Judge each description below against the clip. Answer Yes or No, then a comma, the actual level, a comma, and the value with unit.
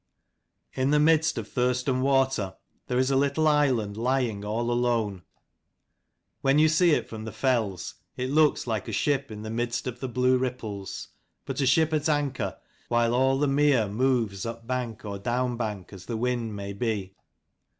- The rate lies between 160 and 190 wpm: Yes, average, 170 wpm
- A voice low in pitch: Yes, low, 125 Hz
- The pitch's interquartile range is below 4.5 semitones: Yes, average, 3.6 semitones